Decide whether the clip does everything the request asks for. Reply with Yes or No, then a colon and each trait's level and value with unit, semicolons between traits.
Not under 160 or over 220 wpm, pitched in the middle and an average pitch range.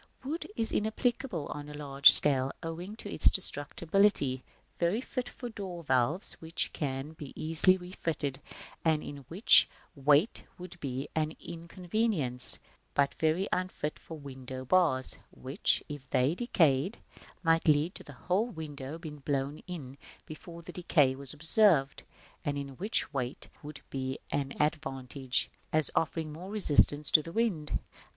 No: average, 145 wpm; medium, 155 Hz; average, 4.4 semitones